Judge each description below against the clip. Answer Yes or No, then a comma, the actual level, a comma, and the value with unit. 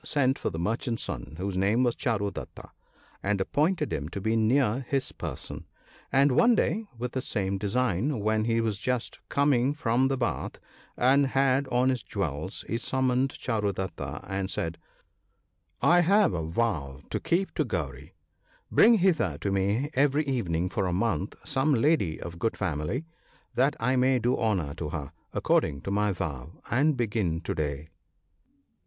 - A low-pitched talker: Yes, low, 115 Hz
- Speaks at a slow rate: No, average, 175 wpm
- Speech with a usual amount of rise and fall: No, wide, 5.9 semitones